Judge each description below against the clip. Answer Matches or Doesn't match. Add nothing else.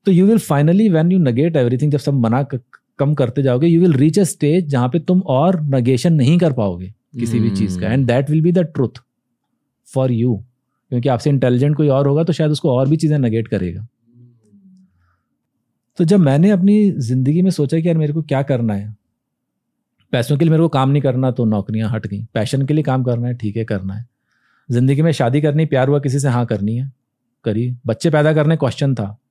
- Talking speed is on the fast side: Matches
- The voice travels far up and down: Doesn't match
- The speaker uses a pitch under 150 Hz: Matches